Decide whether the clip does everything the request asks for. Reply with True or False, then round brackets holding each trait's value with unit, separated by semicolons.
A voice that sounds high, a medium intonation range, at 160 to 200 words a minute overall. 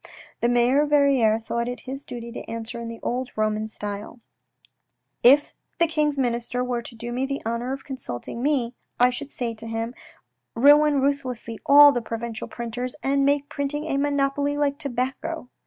True (250 Hz; 3.3 semitones; 180 wpm)